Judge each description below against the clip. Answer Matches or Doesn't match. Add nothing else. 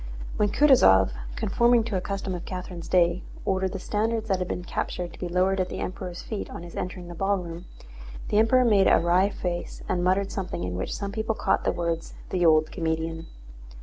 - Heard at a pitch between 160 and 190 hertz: Matches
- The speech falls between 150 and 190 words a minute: Doesn't match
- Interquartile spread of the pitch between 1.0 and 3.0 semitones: Matches